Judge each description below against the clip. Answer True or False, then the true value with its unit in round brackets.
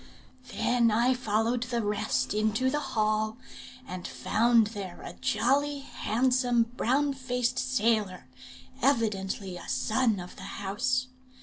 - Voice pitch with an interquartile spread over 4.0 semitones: False (3.4 semitones)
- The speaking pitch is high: True (230 Hz)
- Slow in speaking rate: True (120 wpm)